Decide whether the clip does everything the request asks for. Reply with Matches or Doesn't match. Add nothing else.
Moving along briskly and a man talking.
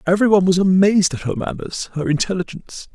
Doesn't match